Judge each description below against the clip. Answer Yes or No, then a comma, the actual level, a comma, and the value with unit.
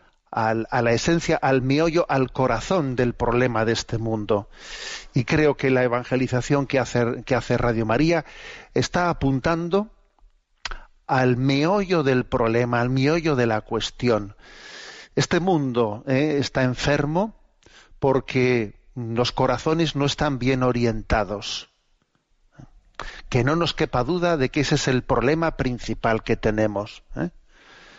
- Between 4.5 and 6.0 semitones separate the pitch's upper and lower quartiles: No, average, 3.9 semitones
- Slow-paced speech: No, average, 135 wpm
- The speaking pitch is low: Yes, low, 130 Hz